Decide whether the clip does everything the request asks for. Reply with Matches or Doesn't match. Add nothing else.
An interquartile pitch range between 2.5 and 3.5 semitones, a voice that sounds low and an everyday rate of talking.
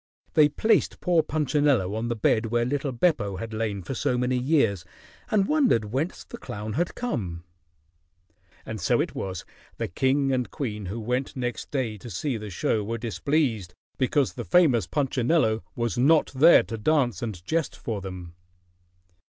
Doesn't match